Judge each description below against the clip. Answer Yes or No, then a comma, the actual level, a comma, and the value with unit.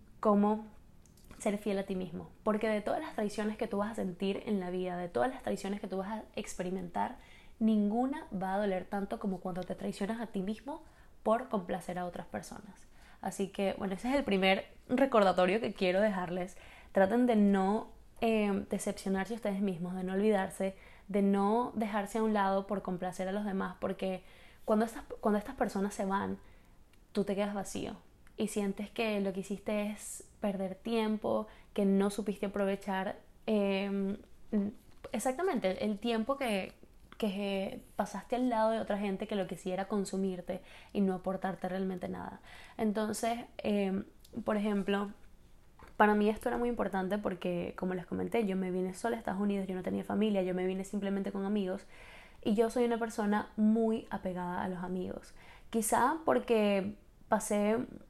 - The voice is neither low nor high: No, high, 205 Hz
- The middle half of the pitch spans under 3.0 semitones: Yes, narrow, 2.4 semitones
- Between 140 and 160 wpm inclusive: No, average, 175 wpm